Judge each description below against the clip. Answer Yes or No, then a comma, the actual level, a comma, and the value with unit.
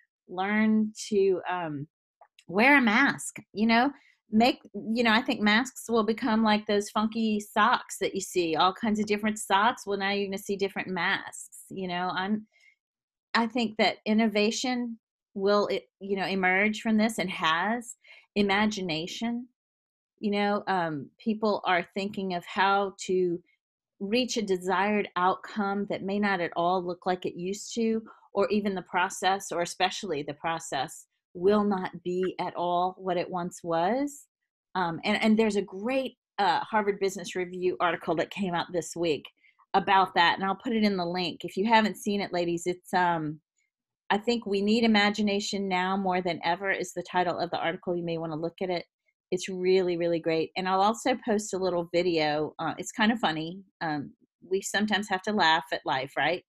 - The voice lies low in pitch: No, high, 195 Hz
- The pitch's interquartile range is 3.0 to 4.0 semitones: Yes, average, 3.3 semitones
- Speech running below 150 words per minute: No, average, 185 wpm